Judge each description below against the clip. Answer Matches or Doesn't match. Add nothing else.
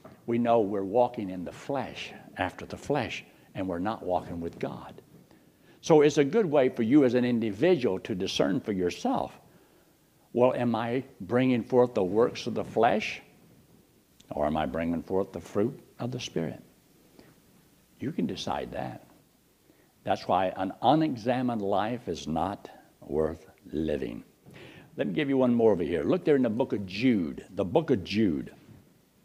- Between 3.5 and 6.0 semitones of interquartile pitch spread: Matches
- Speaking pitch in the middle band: Doesn't match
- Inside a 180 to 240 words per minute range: Doesn't match